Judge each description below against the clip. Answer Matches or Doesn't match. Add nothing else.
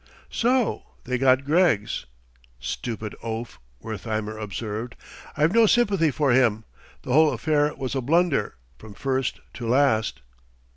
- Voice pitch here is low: Matches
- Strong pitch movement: Matches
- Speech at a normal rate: Doesn't match